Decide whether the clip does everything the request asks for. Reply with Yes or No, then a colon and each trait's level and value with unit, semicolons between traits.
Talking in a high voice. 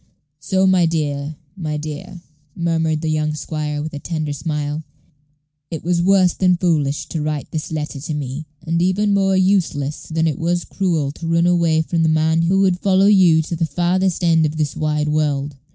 No: medium, 160 Hz